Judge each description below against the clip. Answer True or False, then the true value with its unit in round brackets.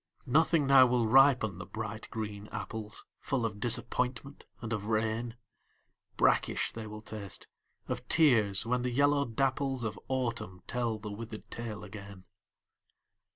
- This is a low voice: True (115 Hz)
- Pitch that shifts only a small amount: False (3.1 semitones)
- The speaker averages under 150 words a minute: True (140 wpm)